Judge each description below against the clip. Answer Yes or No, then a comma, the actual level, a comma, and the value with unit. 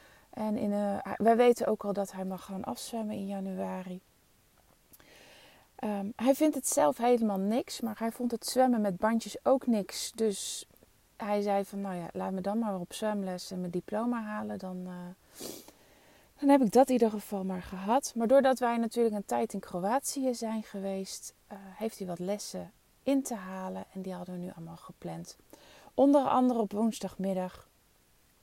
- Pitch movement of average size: Yes, average, 3.8 semitones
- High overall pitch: Yes, high, 210 Hz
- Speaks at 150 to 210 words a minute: Yes, average, 180 wpm